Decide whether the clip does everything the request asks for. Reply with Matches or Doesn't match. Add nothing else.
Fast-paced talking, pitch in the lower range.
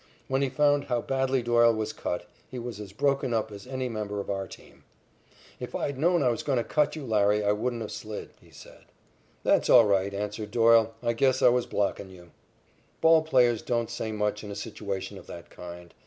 Matches